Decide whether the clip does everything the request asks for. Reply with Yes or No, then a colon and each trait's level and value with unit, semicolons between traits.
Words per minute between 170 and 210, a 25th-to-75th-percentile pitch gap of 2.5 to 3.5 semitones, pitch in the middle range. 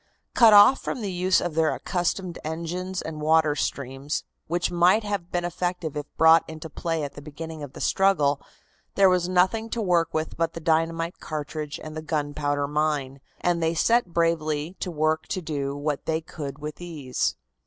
Yes: average, 185 wpm; average, 2.8 semitones; medium, 160 Hz